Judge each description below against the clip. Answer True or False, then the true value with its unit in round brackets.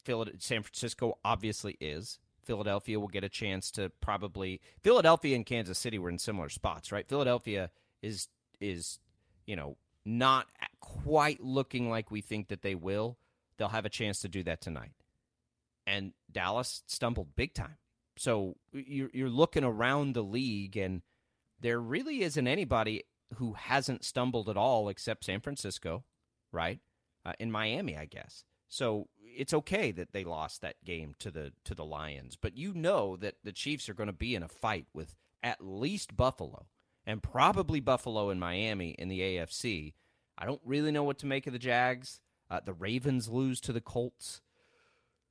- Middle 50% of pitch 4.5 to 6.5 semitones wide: True (4.9 semitones)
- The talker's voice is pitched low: True (105 Hz)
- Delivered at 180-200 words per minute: False (170 wpm)